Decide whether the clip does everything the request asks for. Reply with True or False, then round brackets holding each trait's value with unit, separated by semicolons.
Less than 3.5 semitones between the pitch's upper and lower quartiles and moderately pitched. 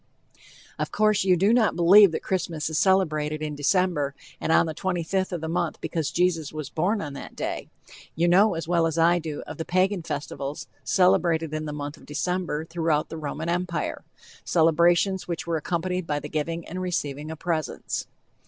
True (2.8 semitones; 165 Hz)